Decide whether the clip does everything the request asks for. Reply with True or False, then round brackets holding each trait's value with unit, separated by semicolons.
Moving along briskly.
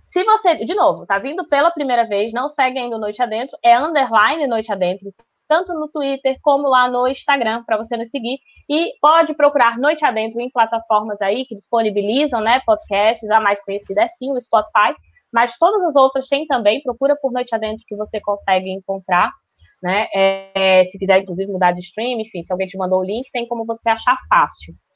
True (195 wpm)